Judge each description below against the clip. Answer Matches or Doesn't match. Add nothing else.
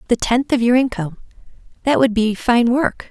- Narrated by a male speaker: Doesn't match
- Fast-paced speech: Doesn't match